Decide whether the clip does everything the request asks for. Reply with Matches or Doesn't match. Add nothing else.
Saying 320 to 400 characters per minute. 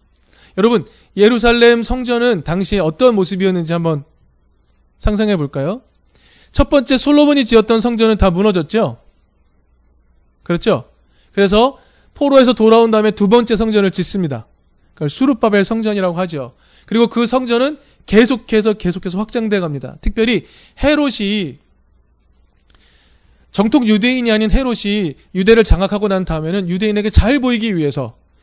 Doesn't match